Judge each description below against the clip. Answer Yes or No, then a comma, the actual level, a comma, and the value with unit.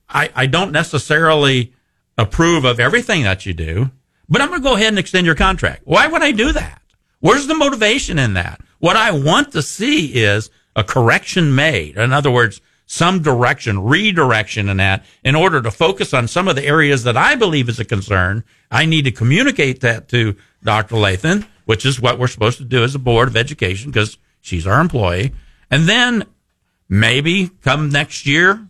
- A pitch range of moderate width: No, wide, 6.7 semitones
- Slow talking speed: No, average, 190 wpm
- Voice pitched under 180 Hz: Yes, low, 135 Hz